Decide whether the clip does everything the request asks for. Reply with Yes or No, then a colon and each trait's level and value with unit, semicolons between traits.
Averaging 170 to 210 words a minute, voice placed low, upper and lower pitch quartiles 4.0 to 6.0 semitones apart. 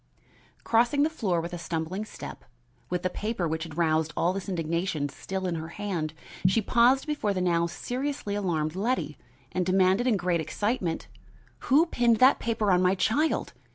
No: average, 175 wpm; medium, 185 Hz; average, 5.3 semitones